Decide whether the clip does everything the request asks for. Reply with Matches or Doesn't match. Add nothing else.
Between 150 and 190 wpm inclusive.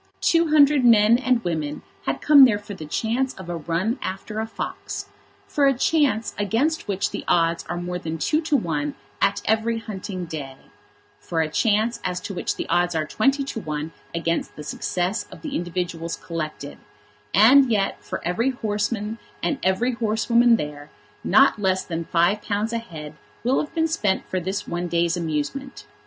Matches